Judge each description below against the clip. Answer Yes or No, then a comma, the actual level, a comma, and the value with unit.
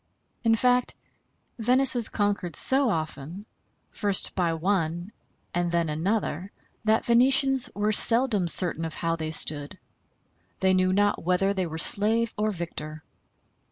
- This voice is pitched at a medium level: No, high, 195 Hz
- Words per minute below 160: Yes, slow, 135 wpm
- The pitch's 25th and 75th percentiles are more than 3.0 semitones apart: Yes, average, 5.1 semitones